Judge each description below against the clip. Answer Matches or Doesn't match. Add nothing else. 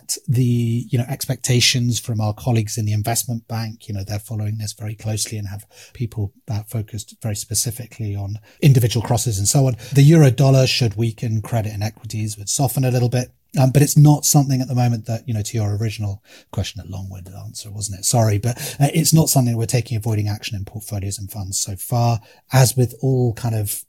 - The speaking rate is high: Matches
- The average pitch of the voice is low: Matches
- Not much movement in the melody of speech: Doesn't match